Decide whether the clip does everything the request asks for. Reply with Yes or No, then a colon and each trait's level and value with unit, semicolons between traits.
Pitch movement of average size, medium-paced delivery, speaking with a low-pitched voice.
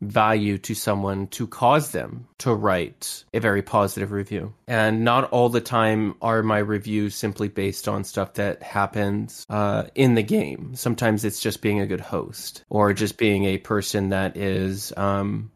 No: narrow, 2.1 semitones; average, 175 wpm; low, 105 Hz